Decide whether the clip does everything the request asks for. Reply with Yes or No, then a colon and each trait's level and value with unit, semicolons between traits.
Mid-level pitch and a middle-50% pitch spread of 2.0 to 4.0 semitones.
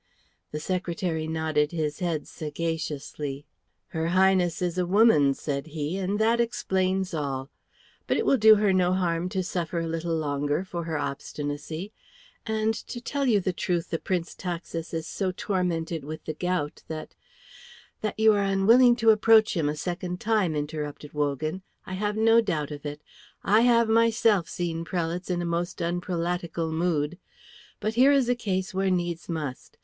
Yes: medium, 175 Hz; average, 3.7 semitones